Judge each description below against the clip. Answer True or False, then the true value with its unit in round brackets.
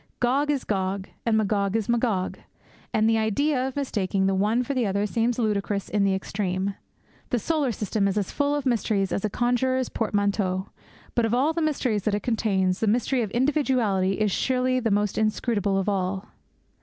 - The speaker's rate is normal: True (190 wpm)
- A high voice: True (215 Hz)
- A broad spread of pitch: False (3.9 semitones)